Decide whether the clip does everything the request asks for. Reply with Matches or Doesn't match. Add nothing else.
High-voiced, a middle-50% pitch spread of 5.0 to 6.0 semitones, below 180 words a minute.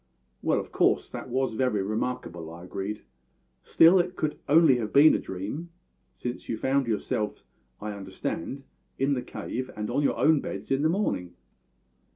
Doesn't match